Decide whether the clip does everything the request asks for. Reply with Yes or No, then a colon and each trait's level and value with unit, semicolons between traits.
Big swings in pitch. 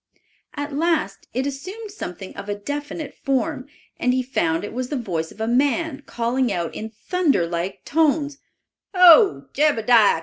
Yes: wide, 6.2 semitones